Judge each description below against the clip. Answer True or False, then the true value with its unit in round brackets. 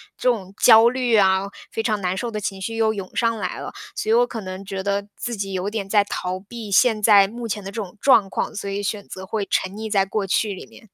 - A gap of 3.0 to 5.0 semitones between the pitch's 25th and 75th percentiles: False (2.5 semitones)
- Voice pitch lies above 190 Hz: True (205 Hz)